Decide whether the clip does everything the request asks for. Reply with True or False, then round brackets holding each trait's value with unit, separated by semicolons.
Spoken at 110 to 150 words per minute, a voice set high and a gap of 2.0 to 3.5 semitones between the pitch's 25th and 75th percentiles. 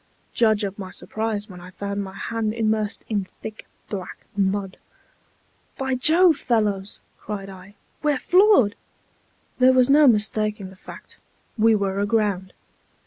True (140 wpm; 210 Hz; 2.8 semitones)